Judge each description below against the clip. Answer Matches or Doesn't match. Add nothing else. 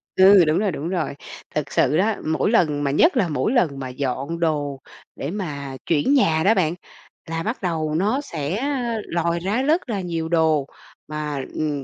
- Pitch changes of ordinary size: Matches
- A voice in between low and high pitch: Matches